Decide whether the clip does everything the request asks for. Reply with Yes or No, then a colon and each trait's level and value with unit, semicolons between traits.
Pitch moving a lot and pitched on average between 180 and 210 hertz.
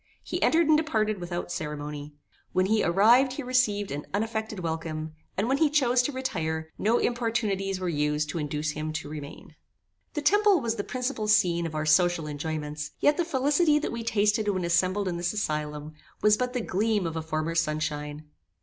Yes: wide, 7.3 semitones; medium, 185 Hz